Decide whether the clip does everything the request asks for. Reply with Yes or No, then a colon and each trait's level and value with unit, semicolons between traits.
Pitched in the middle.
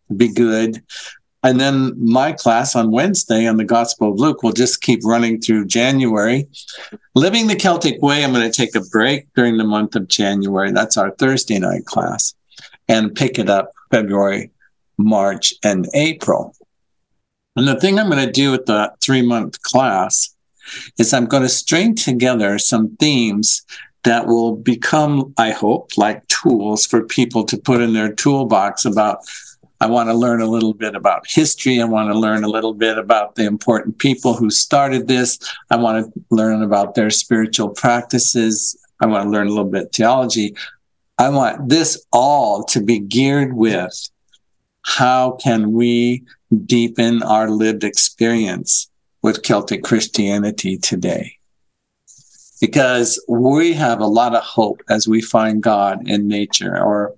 No: low, 115 Hz